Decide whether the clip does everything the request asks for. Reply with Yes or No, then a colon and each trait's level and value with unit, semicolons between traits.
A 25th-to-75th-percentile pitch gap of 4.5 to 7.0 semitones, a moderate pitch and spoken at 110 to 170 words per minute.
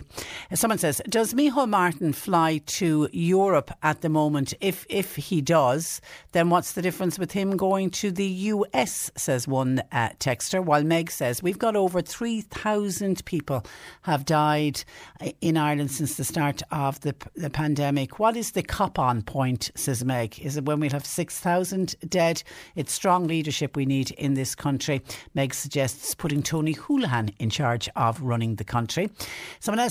Yes: average, 5.1 semitones; medium, 155 Hz; average, 165 wpm